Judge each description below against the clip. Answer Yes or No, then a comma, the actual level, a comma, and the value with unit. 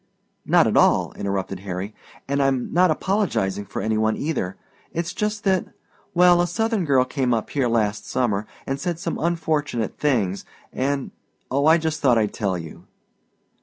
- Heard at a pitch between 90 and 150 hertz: Yes, low, 135 Hz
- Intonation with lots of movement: Yes, wide, 7.9 semitones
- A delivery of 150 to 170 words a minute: Yes, average, 165 wpm